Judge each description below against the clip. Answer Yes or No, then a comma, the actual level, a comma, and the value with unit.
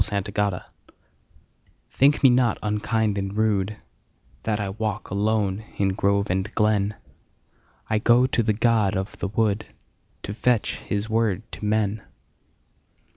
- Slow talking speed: Yes, slow, 125 wpm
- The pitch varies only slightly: Yes, narrow, 1.8 semitones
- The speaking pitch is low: Yes, low, 105 Hz